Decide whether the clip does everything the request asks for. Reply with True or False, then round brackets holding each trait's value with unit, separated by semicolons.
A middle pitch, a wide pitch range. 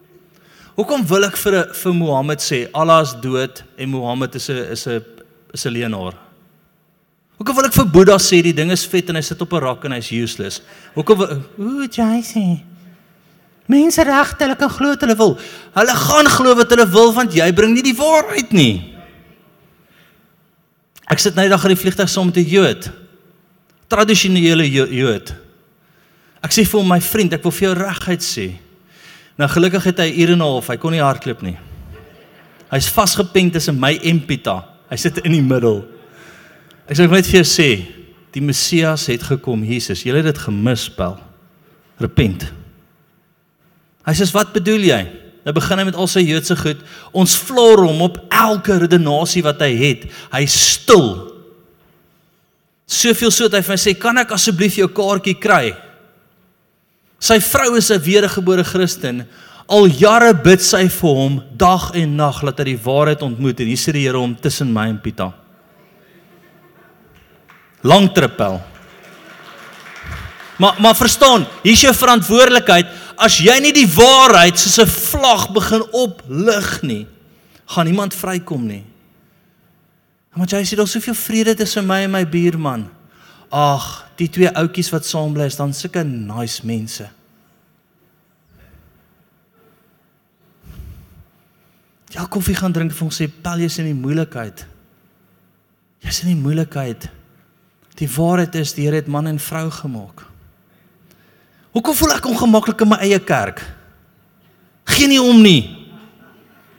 True (175 Hz; 6.2 semitones)